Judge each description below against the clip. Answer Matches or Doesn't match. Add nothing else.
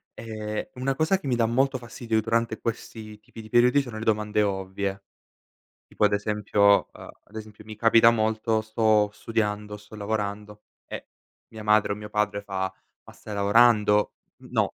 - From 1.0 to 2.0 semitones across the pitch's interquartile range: Matches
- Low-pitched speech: Matches